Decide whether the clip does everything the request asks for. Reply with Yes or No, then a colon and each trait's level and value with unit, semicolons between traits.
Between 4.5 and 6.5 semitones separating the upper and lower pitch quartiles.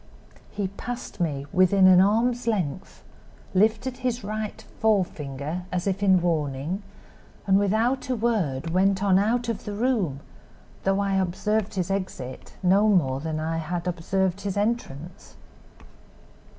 No: average, 3.8 semitones